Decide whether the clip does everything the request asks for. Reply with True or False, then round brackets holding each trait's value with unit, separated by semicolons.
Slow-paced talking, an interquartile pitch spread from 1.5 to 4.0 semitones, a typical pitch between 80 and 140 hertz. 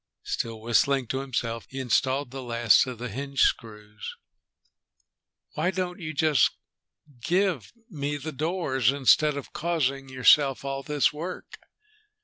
True (130 wpm; 3.5 semitones; 135 Hz)